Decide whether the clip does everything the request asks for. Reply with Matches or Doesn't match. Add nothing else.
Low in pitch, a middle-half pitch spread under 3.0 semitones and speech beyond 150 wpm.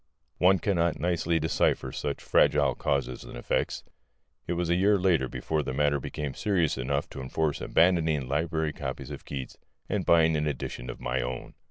Doesn't match